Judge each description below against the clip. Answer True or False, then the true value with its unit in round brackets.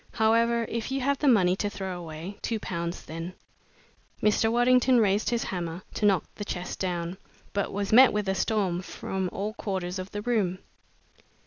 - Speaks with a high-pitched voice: True (200 Hz)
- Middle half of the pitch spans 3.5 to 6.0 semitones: True (3.9 semitones)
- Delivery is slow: False (180 wpm)